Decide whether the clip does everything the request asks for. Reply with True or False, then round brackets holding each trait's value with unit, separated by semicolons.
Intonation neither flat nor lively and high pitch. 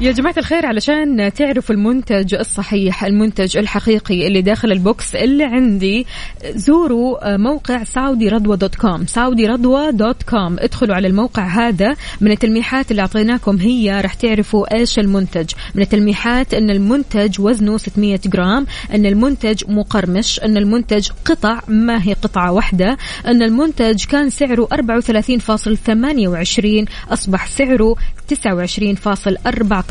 True (3.2 semitones; 220 Hz)